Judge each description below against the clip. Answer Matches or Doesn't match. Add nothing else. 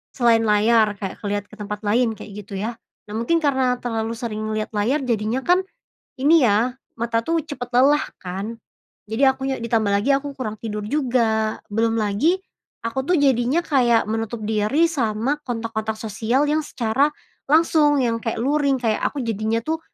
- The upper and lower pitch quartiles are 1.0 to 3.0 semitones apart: Doesn't match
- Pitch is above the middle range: Matches